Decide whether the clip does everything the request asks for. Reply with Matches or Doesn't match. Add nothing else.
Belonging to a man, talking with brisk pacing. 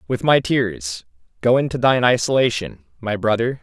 Doesn't match